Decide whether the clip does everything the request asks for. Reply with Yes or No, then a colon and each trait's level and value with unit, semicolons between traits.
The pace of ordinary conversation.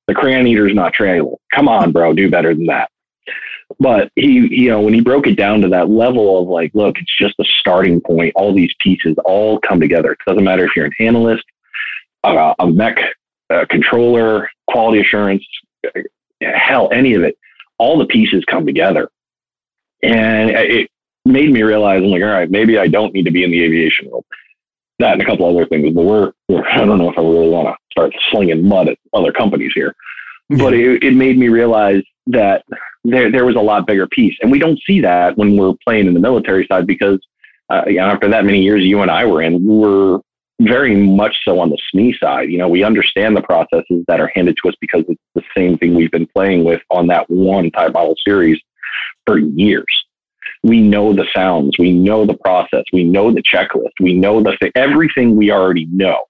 No: fast, 210 wpm